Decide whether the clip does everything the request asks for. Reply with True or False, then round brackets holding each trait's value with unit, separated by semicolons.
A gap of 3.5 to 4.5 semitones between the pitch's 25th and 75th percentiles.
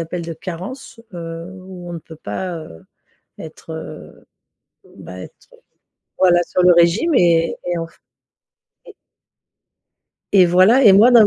False (2.8 semitones)